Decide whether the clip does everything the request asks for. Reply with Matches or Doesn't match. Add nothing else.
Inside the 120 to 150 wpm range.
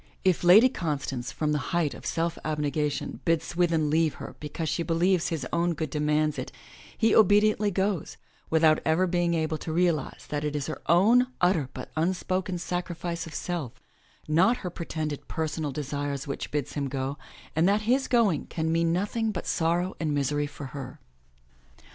Doesn't match